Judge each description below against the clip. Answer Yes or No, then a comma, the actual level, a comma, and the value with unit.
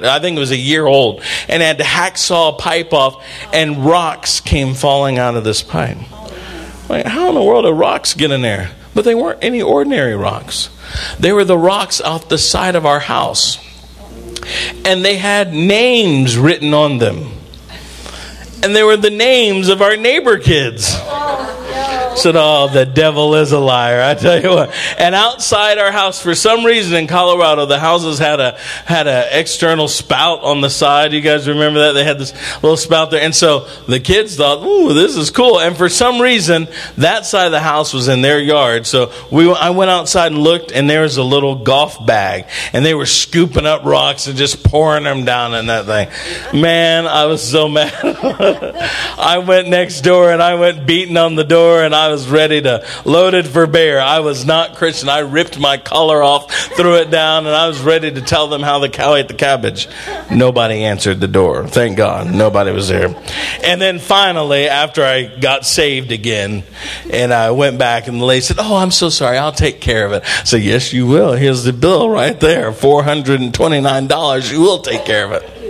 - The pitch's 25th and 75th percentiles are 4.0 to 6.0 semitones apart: Yes, average, 4.4 semitones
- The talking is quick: Yes, fast, 210 wpm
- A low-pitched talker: No, medium, 155 Hz